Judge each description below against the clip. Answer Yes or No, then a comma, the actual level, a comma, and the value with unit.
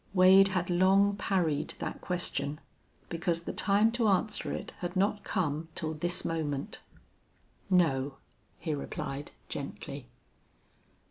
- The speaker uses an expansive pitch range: No, average, 3.8 semitones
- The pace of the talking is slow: Yes, slow, 120 wpm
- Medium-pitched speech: Yes, medium, 175 Hz